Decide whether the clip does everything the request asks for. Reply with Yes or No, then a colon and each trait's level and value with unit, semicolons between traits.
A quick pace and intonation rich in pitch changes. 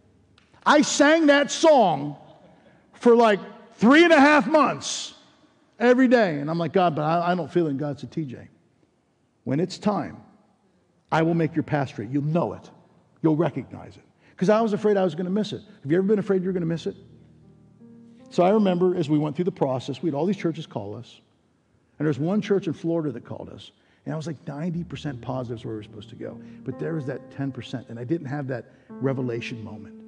Yes: fast, 225 wpm; wide, 7.5 semitones